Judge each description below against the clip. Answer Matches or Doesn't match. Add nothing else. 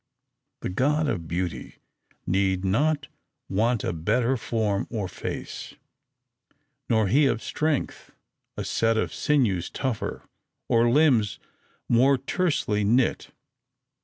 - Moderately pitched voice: Doesn't match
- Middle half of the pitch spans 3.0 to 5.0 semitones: Doesn't match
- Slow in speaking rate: Matches